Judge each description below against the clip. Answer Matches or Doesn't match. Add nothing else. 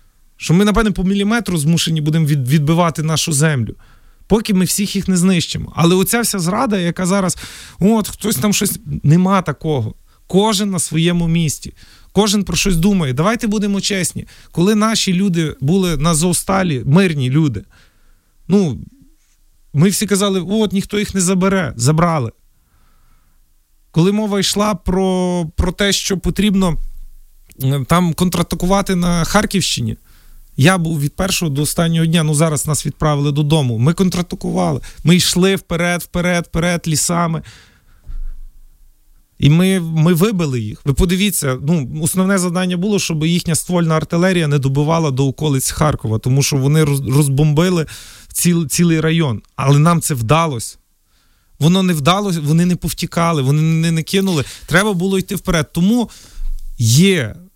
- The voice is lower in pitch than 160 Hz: Doesn't match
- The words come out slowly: Doesn't match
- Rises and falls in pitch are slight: Doesn't match